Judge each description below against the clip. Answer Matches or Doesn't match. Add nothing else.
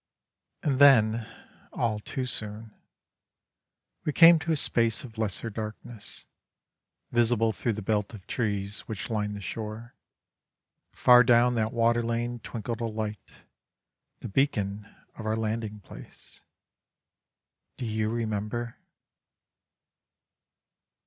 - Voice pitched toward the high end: Doesn't match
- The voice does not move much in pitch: Matches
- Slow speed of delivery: Matches